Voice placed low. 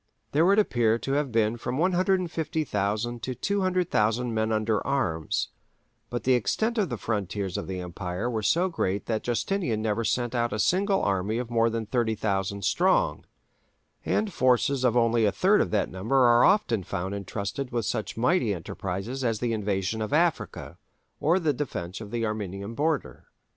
Yes: low, 115 Hz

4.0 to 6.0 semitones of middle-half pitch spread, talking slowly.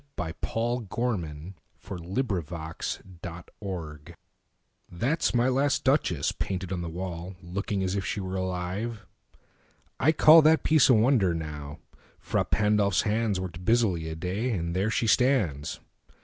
Yes: average, 5.3 semitones; slow, 120 wpm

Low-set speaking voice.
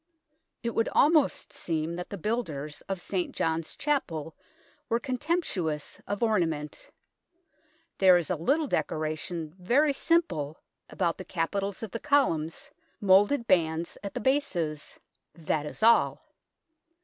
No: medium, 185 Hz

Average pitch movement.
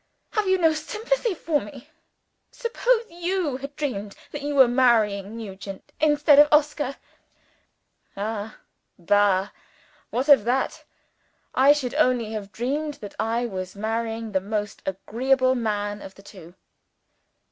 No: wide, 6.1 semitones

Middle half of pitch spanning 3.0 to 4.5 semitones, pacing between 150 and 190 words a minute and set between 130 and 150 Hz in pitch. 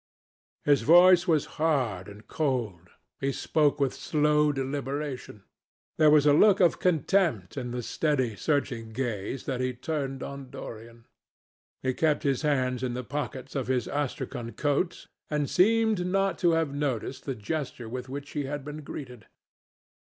Yes: average, 3.3 semitones; average, 155 wpm; medium, 140 Hz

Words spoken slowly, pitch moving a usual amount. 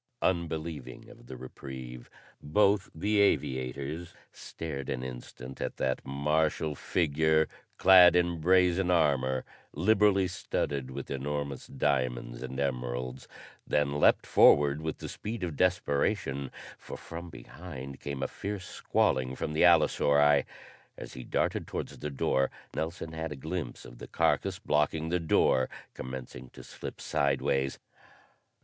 Yes: slow, 130 wpm; average, 4.4 semitones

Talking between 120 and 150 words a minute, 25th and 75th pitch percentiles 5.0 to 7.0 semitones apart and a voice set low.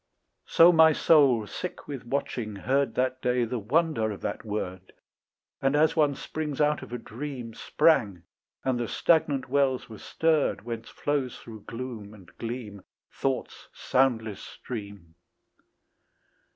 No: average, 140 wpm; average, 4.6 semitones; low, 125 Hz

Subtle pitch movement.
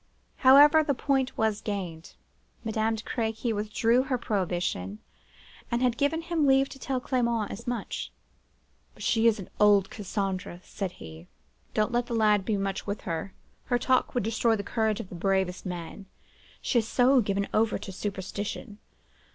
No: average, 3.9 semitones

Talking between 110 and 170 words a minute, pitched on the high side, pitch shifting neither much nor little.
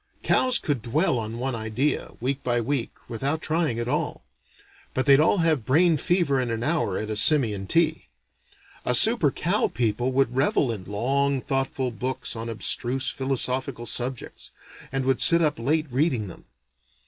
No: average, 165 wpm; low, 130 Hz; average, 3.7 semitones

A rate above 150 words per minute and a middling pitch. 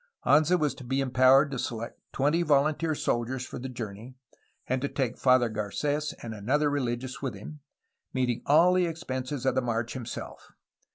No: average, 170 wpm; low, 130 Hz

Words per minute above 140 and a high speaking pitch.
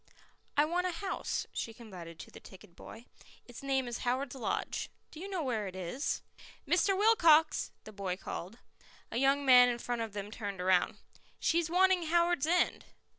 Yes: average, 175 wpm; very high, 255 Hz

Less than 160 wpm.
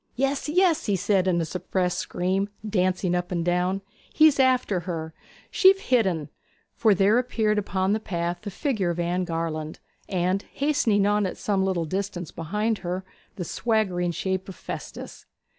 No: average, 165 wpm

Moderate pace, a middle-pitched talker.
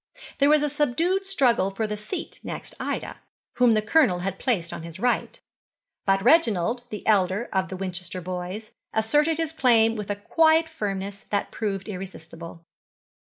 No: average, 165 wpm; high, 215 Hz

